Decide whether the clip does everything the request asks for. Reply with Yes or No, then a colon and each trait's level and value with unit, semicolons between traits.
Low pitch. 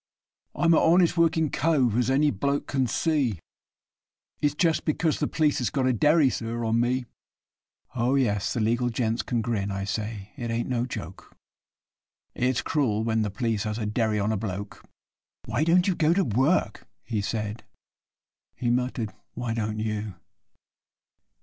Yes: low, 120 Hz